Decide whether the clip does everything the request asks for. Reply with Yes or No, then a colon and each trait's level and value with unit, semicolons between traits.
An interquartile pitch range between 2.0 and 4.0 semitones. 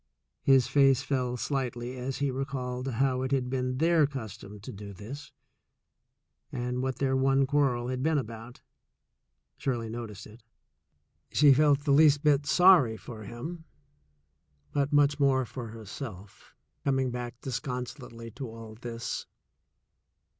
Yes: average, 2.7 semitones